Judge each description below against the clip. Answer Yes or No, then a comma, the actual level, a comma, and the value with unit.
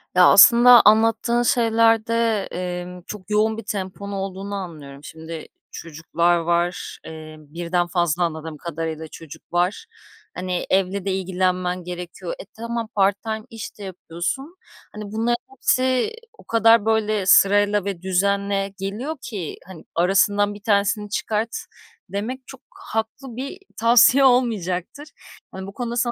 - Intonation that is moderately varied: Yes, average, 4.2 semitones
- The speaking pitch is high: Yes, high, 200 Hz